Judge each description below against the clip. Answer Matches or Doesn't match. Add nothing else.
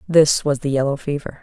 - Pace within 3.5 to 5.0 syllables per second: Doesn't match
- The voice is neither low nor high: Matches